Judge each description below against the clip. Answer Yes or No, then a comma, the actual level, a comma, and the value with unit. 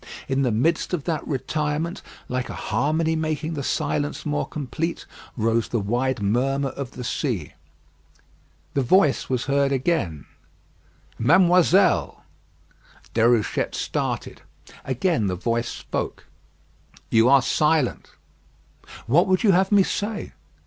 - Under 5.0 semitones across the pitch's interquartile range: No, average, 5.3 semitones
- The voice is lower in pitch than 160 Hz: Yes, medium, 140 Hz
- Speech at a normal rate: No, slow, 120 wpm